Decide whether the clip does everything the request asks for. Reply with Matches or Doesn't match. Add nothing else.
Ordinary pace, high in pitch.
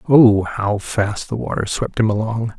Doesn't match